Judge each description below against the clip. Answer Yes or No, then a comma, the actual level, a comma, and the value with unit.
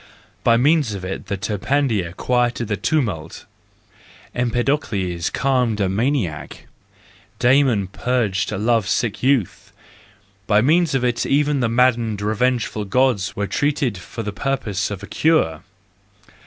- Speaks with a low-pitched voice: Yes, low, 115 Hz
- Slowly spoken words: Yes, slow, 130 wpm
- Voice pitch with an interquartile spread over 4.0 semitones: Yes, average, 4.5 semitones